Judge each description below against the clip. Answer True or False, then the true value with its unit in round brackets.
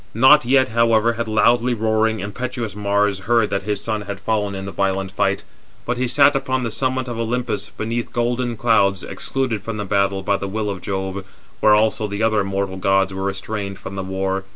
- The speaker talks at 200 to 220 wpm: True (205 wpm)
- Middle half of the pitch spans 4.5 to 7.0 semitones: False (3.2 semitones)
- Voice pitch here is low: True (105 Hz)